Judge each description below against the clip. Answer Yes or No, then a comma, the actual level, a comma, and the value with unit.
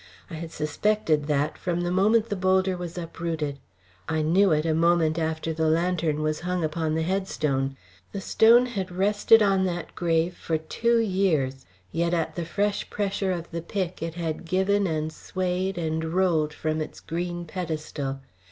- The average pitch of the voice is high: No, medium, 170 Hz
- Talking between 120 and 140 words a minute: No, average, 170 wpm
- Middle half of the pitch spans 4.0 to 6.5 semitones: No, average, 3.1 semitones